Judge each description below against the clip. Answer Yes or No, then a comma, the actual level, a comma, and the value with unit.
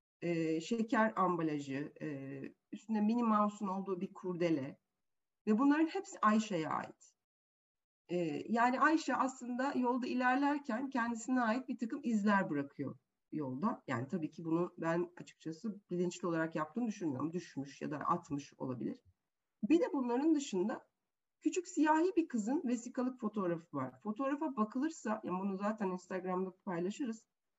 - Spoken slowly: No, average, 135 wpm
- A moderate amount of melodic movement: No, wide, 6.8 semitones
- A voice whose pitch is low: No, high, 210 Hz